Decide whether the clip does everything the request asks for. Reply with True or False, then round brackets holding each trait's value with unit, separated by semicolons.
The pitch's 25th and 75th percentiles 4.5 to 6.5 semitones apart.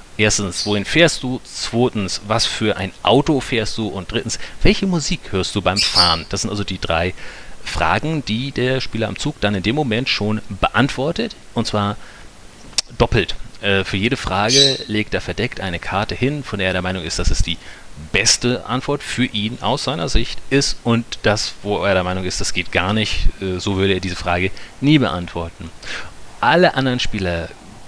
True (4.9 semitones)